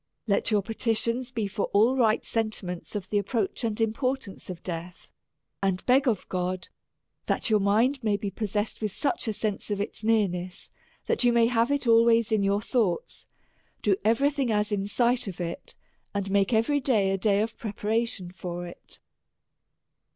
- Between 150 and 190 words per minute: Yes, average, 180 wpm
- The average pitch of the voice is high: Yes, high, 215 Hz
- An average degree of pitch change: Yes, average, 3.0 semitones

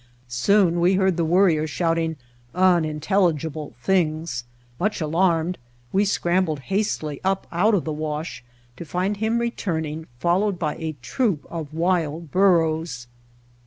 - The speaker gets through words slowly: Yes, slow, 130 wpm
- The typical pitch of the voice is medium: Yes, medium, 170 Hz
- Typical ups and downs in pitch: Yes, average, 3.3 semitones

